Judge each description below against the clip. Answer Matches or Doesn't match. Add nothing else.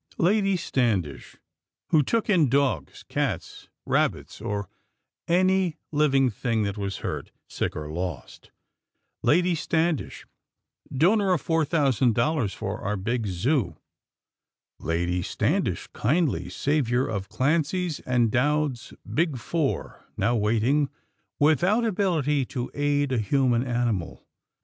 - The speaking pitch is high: Doesn't match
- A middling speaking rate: Doesn't match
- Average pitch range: Doesn't match